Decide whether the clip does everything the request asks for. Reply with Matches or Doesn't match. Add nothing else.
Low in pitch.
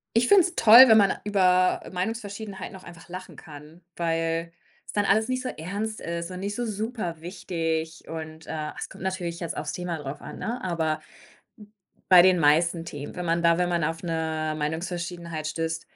Doesn't match